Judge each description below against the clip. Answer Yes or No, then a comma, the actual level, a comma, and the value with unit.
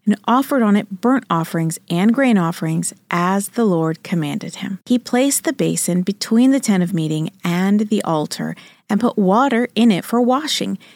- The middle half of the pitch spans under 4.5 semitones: No, average, 5.2 semitones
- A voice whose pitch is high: Yes, high, 205 Hz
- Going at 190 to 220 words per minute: No, average, 180 wpm